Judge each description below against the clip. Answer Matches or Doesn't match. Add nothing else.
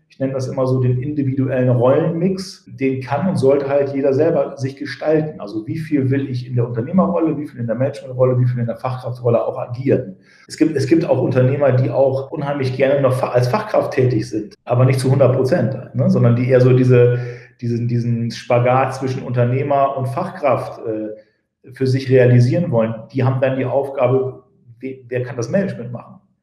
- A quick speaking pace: Matches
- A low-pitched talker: Matches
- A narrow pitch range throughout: Matches